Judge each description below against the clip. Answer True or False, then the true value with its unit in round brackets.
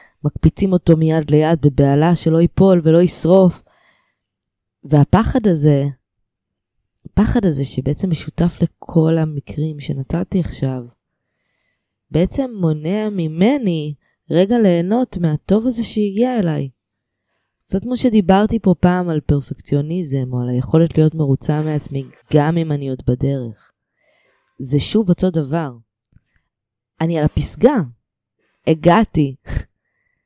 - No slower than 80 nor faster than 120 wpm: True (105 wpm)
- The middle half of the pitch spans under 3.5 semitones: False (4.8 semitones)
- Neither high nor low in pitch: True (160 Hz)